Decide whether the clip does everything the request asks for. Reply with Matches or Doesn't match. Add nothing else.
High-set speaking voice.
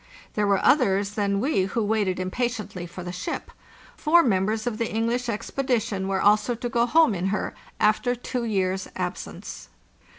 Matches